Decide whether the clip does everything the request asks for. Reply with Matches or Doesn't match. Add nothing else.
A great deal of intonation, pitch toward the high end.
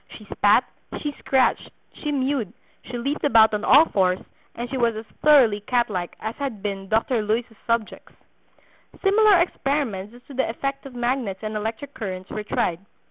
Doesn't match